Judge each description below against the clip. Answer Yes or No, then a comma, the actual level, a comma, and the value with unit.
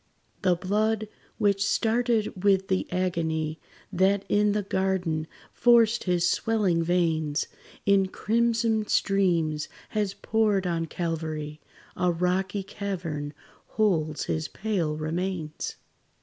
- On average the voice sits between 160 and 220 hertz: Yes, medium, 185 Hz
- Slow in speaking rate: Yes, slow, 105 wpm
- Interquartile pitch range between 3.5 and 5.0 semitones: Yes, average, 4.0 semitones